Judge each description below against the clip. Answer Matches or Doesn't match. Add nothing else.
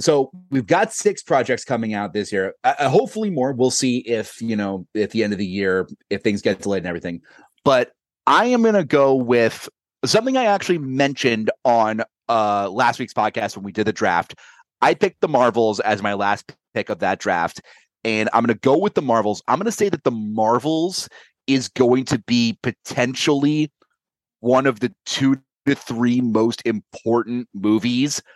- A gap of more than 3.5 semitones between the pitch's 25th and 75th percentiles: Matches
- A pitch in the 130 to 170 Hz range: Doesn't match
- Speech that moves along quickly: Doesn't match